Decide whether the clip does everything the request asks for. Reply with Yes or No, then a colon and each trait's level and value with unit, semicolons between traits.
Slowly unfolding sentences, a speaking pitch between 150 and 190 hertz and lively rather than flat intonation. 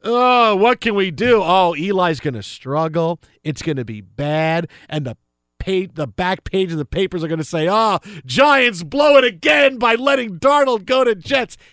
No: average, 200 wpm; medium, 185 Hz; wide, 7.3 semitones